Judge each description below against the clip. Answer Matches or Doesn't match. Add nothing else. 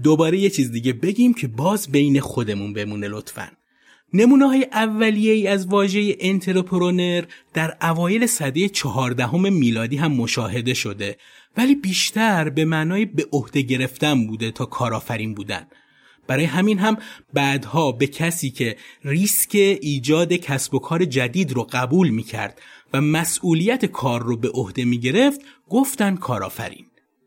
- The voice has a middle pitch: Matches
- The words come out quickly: Doesn't match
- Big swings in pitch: Matches